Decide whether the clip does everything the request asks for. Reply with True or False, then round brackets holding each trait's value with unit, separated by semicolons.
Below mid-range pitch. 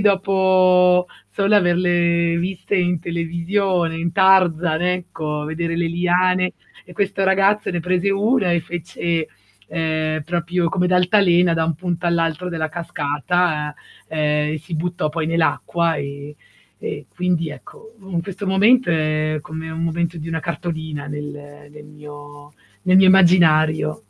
False (170 Hz)